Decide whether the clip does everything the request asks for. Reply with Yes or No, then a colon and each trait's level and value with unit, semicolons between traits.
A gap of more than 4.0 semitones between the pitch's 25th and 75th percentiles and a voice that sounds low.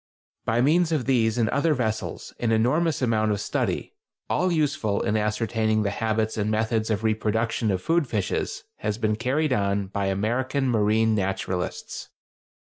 No: average, 3.2 semitones; low, 110 Hz